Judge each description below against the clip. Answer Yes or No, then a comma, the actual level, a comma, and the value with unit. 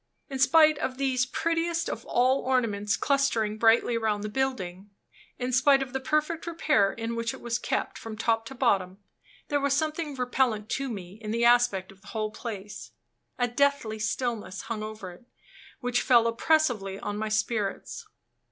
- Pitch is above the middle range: Yes, high, 235 Hz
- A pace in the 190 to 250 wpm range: No, average, 170 wpm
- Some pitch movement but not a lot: Yes, average, 4.0 semitones